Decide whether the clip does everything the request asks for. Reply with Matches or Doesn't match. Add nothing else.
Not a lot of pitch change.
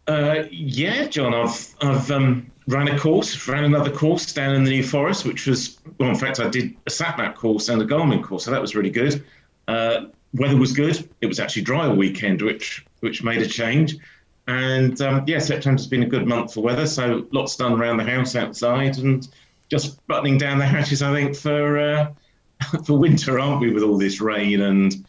Doesn't match